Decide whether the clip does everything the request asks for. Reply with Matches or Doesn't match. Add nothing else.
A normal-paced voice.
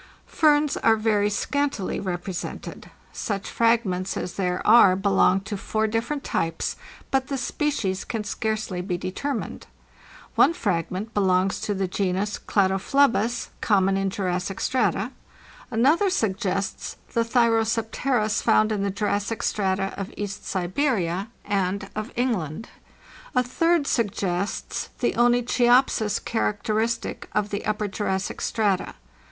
Doesn't match